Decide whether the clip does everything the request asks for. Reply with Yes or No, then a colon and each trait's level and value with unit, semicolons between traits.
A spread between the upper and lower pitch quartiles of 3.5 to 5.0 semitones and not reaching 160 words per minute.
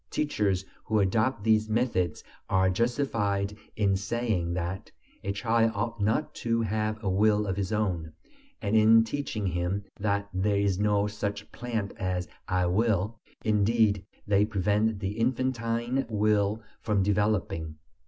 No: narrow, 2.4 semitones; average, 140 wpm